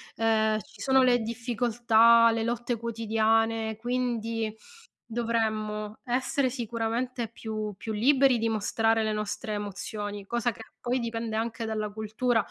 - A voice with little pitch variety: Yes, narrow, 1.6 semitones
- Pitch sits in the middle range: No, high, 225 Hz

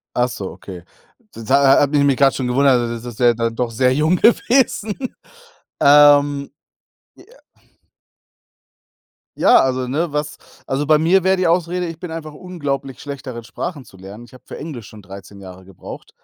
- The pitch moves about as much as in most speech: Yes, average, 4.6 semitones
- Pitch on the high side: No, medium, 140 Hz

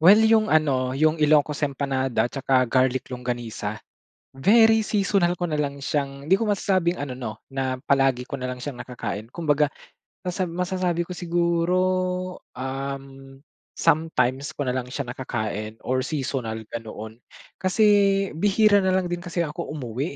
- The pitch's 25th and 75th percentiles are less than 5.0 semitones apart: No, average, 5.3 semitones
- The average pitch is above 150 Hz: No, medium, 140 Hz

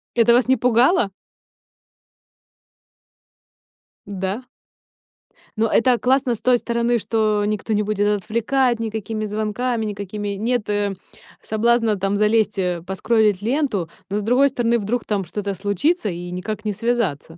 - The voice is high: Yes, high, 215 Hz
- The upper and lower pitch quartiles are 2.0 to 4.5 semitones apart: Yes, average, 2.7 semitones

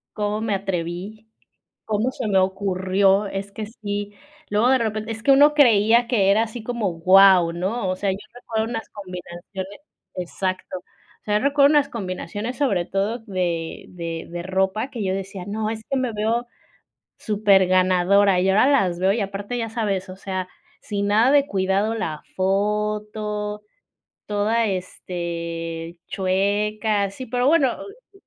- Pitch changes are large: No, average, 2.9 semitones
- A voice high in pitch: Yes, high, 205 Hz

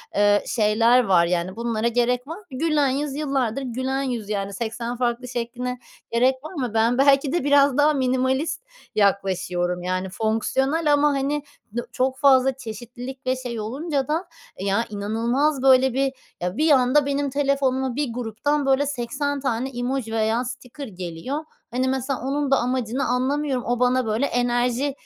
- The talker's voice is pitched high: Yes, very high, 255 Hz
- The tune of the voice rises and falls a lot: No, average, 3.1 semitones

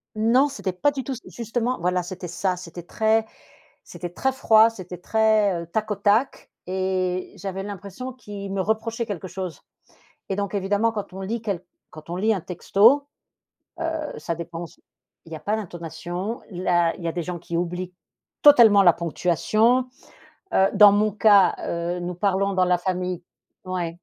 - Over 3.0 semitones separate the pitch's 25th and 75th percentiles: Yes, average, 3.5 semitones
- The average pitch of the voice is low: No, high, 195 Hz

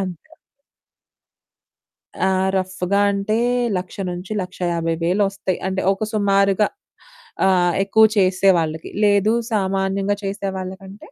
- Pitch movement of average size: No, narrow, 1.5 semitones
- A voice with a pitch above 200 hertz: No, high, 190 Hz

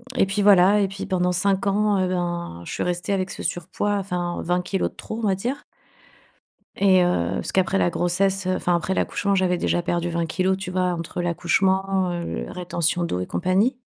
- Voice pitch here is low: No, medium, 185 Hz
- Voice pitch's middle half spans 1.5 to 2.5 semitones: Yes, narrow, 1.9 semitones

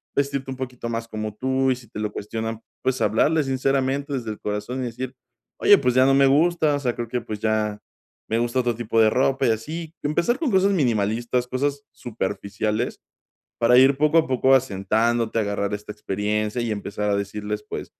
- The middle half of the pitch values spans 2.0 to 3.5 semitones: No, average, 4.0 semitones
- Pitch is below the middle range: Yes, low, 120 Hz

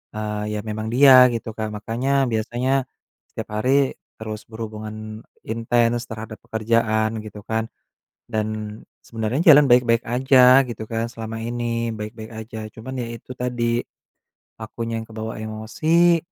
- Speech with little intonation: Yes, narrow, 2.0 semitones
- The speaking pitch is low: Yes, low, 115 Hz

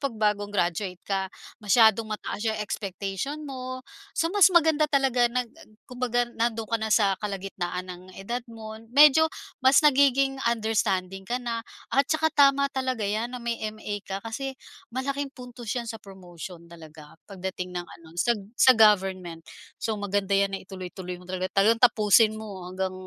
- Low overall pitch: No, high, 220 Hz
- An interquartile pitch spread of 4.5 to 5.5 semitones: Yes, average, 4.9 semitones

